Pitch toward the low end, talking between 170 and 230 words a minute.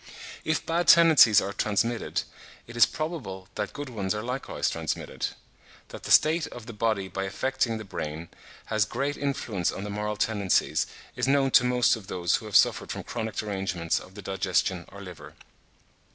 Yes: low, 110 Hz; average, 180 wpm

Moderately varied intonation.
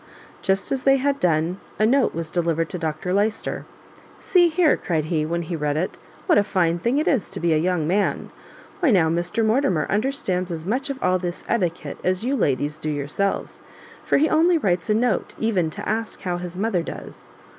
No: wide, 5.7 semitones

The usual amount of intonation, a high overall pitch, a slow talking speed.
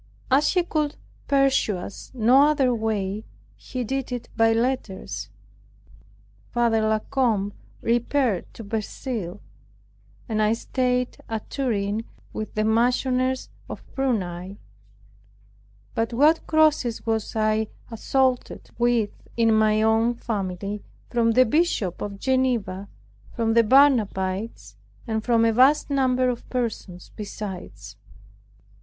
Yes: average, 3.2 semitones; high, 230 Hz; slow, 115 wpm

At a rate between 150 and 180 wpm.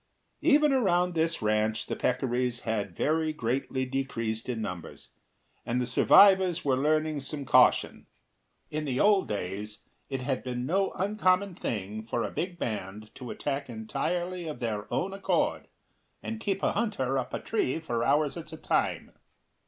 Yes: average, 160 wpm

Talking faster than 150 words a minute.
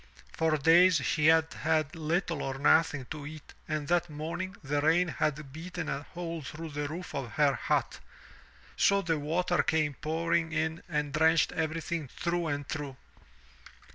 Yes: average, 160 wpm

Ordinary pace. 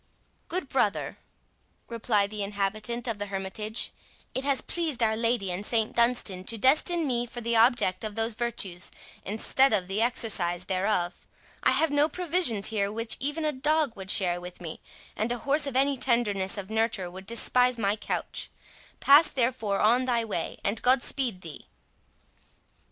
Yes: average, 165 wpm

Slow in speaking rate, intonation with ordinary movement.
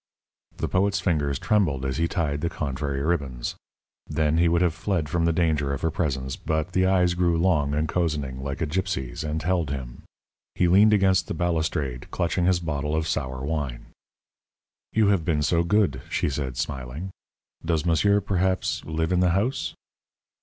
No: average, 175 wpm; average, 4.0 semitones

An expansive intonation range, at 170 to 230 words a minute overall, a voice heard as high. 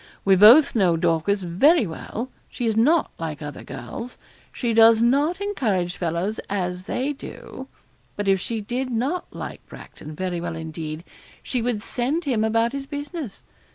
No: wide, 6.6 semitones; average, 160 wpm; high, 220 Hz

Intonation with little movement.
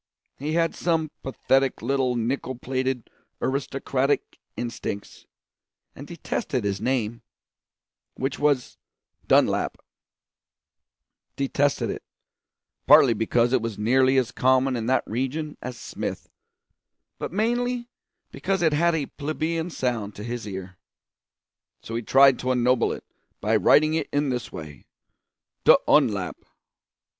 No: average, 3.7 semitones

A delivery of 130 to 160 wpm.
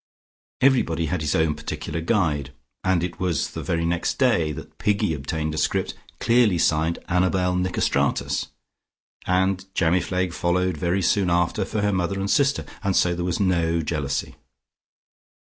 Yes: average, 150 wpm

